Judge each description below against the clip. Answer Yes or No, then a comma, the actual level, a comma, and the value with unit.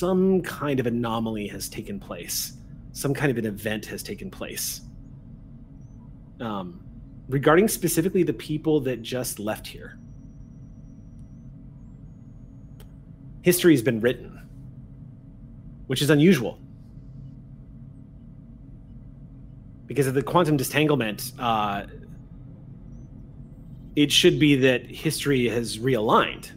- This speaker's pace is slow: Yes, slow, 100 wpm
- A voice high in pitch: No, low, 130 Hz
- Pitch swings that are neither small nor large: No, narrow, 2.2 semitones